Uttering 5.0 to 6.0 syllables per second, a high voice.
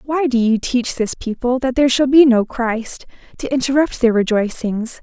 No: 4.8 syllables/s; very high, 250 Hz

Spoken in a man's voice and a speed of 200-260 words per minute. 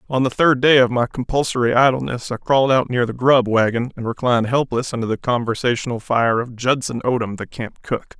Yes: male; fast, 205 wpm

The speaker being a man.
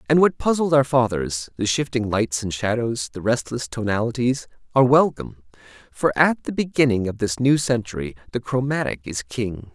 Yes: male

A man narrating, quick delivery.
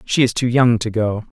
Yes: male; fast, 260 wpm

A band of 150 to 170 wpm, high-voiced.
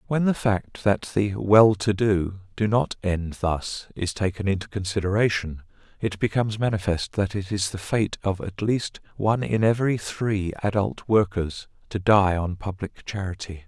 No: average, 165 wpm; low, 100 Hz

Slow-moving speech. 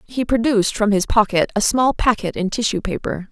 No: average, 200 wpm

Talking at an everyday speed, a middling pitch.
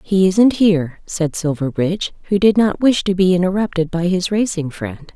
Yes: average, 185 wpm; medium, 180 Hz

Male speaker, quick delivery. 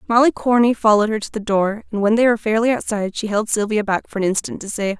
No: female; fast, 265 wpm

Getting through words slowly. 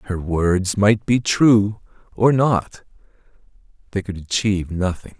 Yes: slow, 125 wpm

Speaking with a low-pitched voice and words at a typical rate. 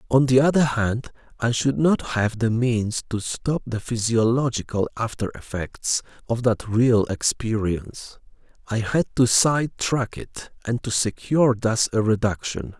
Yes: low, 120 Hz; average, 145 wpm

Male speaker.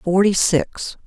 No: female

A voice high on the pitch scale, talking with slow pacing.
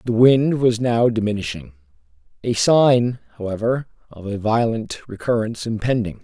No: low, 110 Hz; slow, 115 wpm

